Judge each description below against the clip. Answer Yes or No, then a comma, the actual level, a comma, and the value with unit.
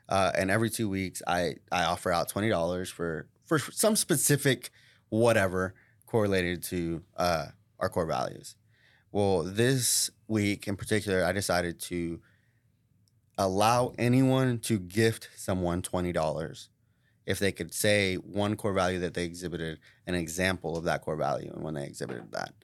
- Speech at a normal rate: Yes, average, 155 wpm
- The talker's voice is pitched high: No, low, 100 Hz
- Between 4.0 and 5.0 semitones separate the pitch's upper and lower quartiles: Yes, average, 4.3 semitones